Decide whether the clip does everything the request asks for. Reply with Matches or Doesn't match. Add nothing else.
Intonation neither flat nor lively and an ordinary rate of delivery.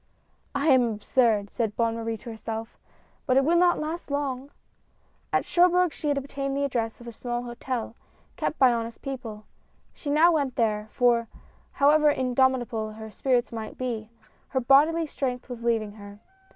Matches